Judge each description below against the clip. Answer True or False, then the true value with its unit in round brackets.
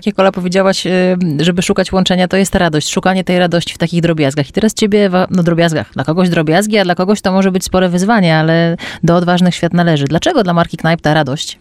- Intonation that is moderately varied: False (2.1 semitones)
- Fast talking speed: True (220 wpm)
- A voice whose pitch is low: False (180 Hz)